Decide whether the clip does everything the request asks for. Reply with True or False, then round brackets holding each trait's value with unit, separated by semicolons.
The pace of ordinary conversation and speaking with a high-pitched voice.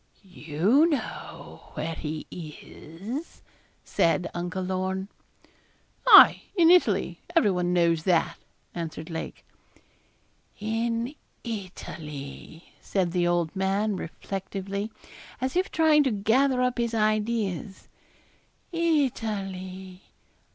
False (95 wpm; 195 Hz)